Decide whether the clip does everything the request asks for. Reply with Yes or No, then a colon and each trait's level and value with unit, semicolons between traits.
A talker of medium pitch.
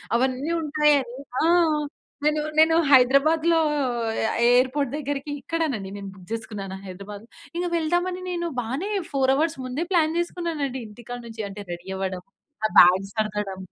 No: very high, 265 Hz